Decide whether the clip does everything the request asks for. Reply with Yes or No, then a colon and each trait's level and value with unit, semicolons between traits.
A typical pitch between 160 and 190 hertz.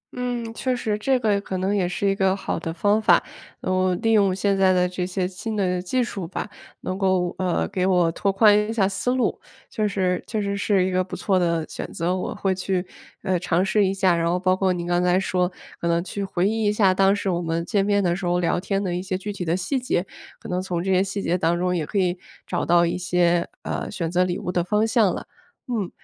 Yes: medium, 185 Hz